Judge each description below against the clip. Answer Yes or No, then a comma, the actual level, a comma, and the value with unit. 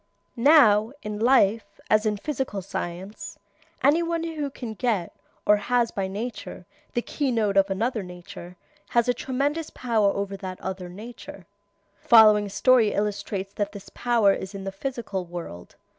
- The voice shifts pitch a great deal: No, average, 3.8 semitones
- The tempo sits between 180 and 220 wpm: No, average, 160 wpm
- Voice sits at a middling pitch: No, high, 210 Hz